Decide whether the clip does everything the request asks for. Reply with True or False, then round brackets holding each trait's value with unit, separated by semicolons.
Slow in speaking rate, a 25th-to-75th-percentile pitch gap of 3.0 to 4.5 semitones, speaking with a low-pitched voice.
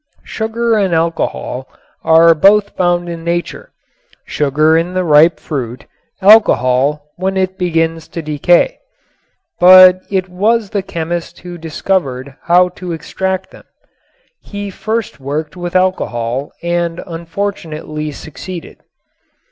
False (115 wpm; 3.4 semitones; 170 Hz)